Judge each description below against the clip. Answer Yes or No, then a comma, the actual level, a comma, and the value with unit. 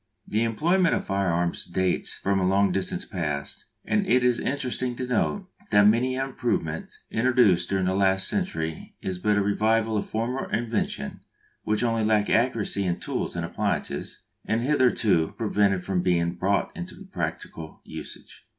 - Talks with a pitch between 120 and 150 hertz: No, low, 105 Hz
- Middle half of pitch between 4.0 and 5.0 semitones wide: Yes, average, 4.6 semitones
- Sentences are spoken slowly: No, average, 165 wpm